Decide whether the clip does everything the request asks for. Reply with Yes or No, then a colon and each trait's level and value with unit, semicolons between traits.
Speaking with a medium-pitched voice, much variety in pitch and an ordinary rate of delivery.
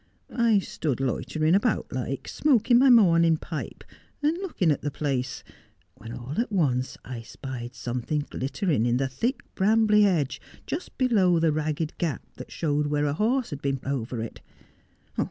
Yes: medium, 155 Hz; wide, 7.5 semitones; average, 160 wpm